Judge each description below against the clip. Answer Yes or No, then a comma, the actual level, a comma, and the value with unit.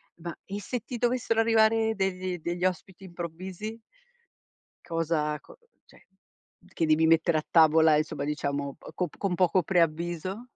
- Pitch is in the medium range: Yes, medium, 175 Hz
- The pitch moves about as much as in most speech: Yes, average, 3.4 semitones